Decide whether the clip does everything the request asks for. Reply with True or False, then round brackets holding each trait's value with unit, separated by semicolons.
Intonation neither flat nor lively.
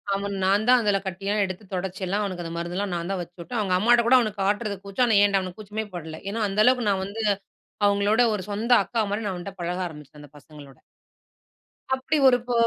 True (3.1 semitones)